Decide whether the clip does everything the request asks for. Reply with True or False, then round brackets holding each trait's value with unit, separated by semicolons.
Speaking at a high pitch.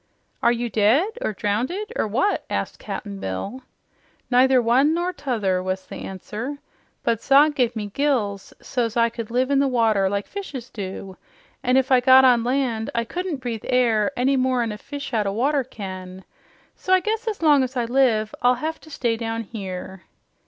True (245 Hz)